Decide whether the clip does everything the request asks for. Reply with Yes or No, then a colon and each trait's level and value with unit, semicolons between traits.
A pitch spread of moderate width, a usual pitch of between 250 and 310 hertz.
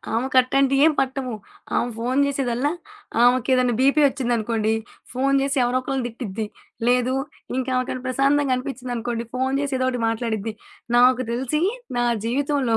No: narrow, 2.0 semitones; very high, 255 Hz